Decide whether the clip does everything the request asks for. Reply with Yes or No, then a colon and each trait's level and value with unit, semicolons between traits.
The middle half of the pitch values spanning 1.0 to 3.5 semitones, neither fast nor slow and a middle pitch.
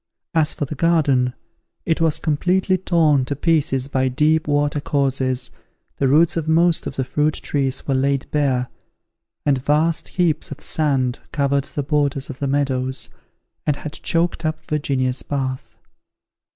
Yes: average, 2.8 semitones; average, 150 wpm; medium, 145 Hz